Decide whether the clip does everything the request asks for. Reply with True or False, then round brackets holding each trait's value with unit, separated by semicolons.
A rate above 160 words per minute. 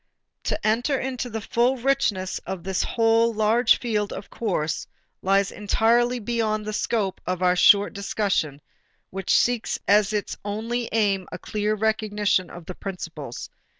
False (150 wpm)